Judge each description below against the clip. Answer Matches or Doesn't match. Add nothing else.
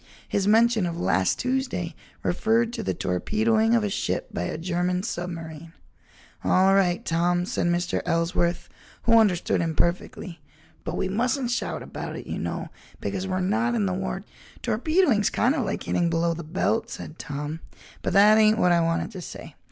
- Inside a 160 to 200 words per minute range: Matches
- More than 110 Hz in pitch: Matches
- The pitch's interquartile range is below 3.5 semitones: Doesn't match